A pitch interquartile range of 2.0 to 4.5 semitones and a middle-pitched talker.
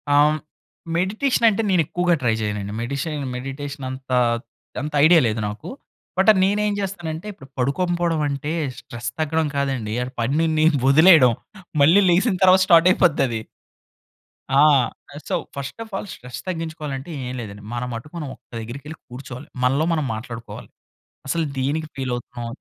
No: average, 5.2 semitones; medium, 145 Hz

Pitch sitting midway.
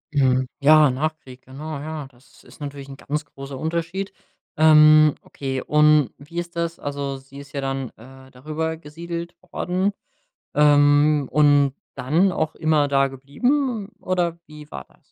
Yes: medium, 150 Hz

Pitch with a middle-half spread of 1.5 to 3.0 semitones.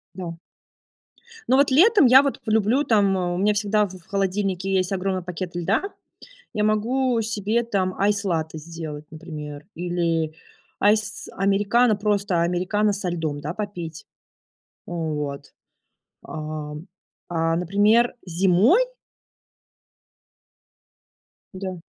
No: average, 3.9 semitones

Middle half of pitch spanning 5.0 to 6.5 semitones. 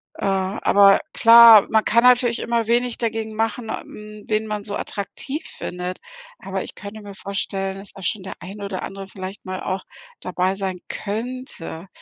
No: average, 2.7 semitones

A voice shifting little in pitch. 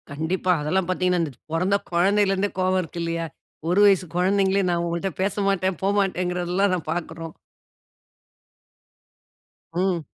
Yes: narrow, 2.2 semitones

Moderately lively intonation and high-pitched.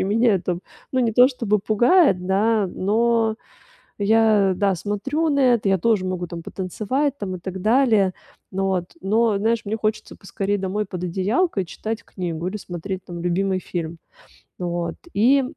Yes: average, 3.4 semitones; high, 200 Hz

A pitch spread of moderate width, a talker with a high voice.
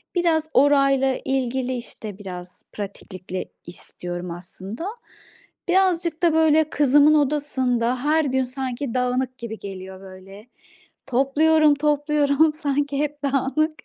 Yes: average, 4.4 semitones; very high, 270 Hz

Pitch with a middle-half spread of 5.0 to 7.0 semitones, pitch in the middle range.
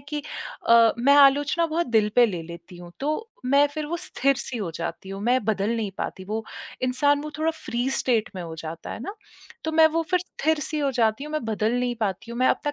No: wide, 5.5 semitones; very high, 250 Hz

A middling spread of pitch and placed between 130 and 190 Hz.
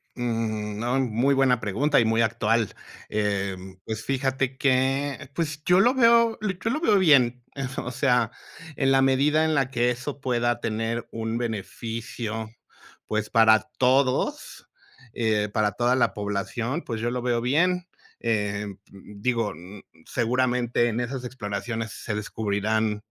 No: average, 3.4 semitones; low, 120 Hz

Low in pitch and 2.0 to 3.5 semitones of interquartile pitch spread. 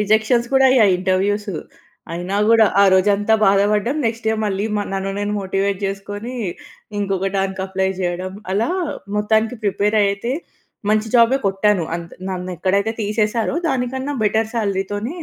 No: high, 205 Hz; narrow, 2.4 semitones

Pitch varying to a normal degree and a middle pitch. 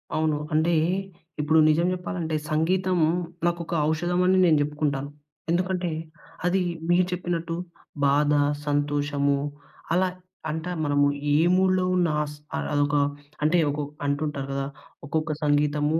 Yes: average, 3.2 semitones; medium, 155 Hz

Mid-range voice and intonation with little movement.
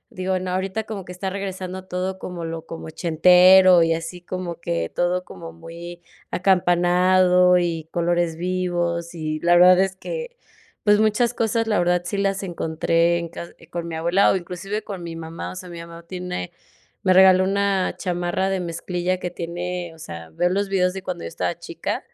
Yes: medium, 180 Hz; narrow, 1.8 semitones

